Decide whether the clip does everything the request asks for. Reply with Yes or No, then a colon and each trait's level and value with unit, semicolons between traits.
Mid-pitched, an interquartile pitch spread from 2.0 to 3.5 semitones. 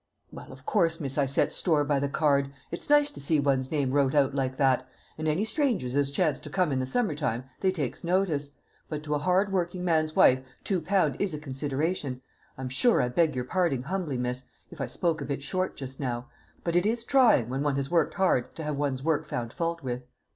No: medium, 150 Hz; average, 4.6 semitones